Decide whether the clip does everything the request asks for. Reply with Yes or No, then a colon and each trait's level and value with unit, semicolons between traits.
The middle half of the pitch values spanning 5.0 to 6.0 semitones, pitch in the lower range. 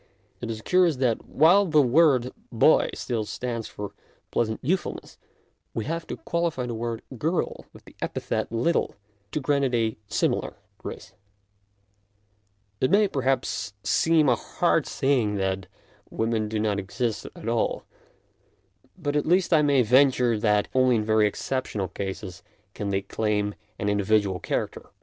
Yes: average, 5.3 semitones; low, 120 Hz